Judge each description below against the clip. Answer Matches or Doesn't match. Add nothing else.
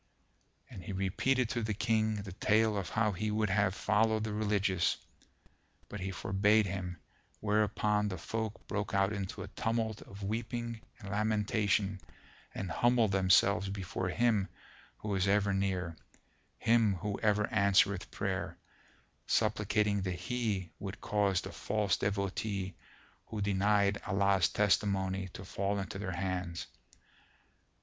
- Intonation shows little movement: Matches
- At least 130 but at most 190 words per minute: Matches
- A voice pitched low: Matches